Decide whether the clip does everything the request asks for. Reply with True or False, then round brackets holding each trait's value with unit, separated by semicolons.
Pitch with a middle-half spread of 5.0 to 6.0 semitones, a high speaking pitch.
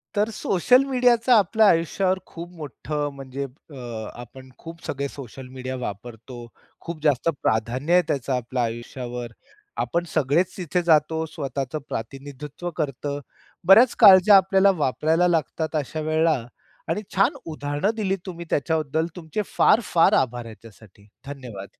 False (5.3 semitones; 150 Hz)